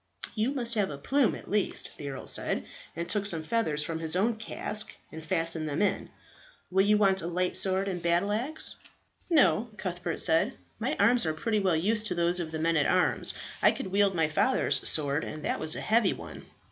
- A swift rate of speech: Yes, fast, 210 wpm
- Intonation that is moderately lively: Yes, average, 4.7 semitones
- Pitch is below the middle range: No, medium, 185 Hz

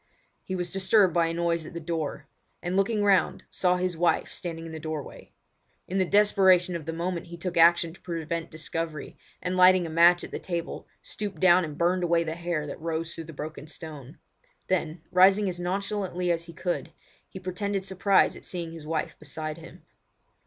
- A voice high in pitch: No, medium, 170 Hz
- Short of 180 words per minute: No, average, 195 wpm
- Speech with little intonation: Yes, narrow, 2.2 semitones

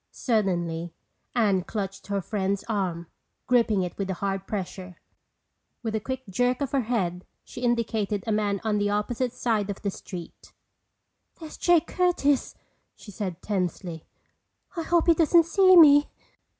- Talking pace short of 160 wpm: Yes, average, 150 wpm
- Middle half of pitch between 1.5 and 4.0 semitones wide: No, average, 4.7 semitones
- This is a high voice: Yes, high, 210 Hz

